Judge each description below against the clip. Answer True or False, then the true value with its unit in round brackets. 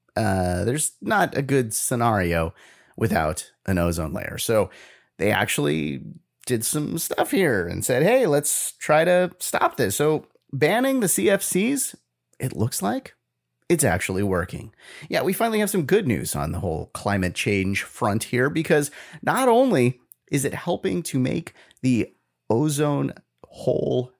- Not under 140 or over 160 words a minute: True (150 wpm)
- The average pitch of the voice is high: False (130 Hz)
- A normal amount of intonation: False (7.6 semitones)